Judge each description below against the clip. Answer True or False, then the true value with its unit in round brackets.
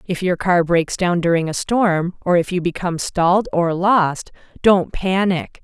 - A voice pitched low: False (180 Hz)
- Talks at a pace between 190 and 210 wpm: False (180 wpm)